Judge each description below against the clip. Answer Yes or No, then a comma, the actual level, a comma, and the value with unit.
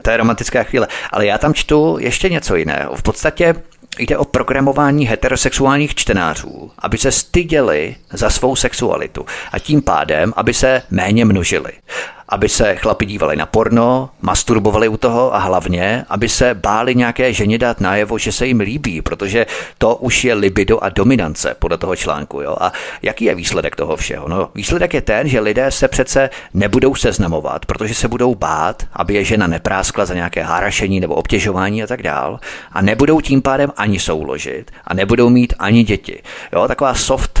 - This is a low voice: Yes, low, 115 Hz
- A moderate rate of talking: No, fast, 175 wpm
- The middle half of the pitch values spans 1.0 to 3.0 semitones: No, average, 4.6 semitones